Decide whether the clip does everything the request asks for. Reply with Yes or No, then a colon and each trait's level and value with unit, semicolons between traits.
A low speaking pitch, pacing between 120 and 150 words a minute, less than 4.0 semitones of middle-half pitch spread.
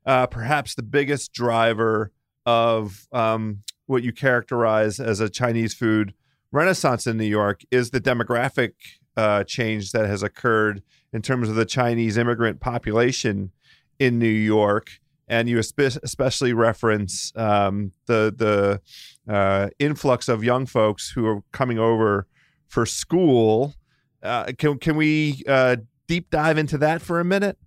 Yes: low, 115 Hz; average, 145 wpm; average, 3.5 semitones